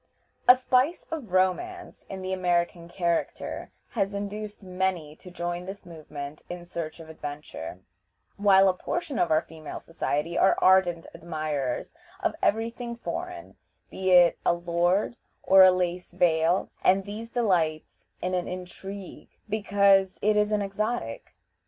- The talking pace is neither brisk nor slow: Yes, average, 145 wpm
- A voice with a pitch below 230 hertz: Yes, medium, 185 Hz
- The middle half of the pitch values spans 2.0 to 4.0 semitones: Yes, average, 3.1 semitones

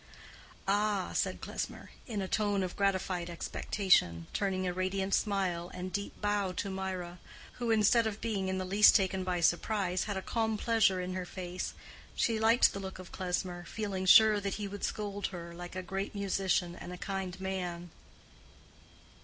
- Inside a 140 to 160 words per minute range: No, average, 175 wpm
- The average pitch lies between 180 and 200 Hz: Yes, high, 190 Hz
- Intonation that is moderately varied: No, narrow, 2.1 semitones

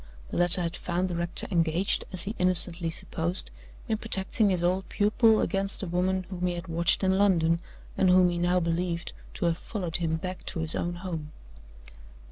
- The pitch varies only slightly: Yes, narrow, 1.9 semitones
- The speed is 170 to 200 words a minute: Yes, average, 190 wpm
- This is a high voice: No, medium, 180 Hz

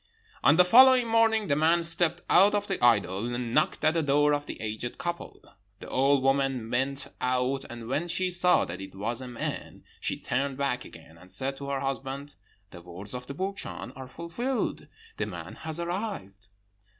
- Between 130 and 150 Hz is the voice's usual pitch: Yes, medium, 140 Hz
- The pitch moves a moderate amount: No, wide, 6.0 semitones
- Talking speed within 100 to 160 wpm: No, average, 190 wpm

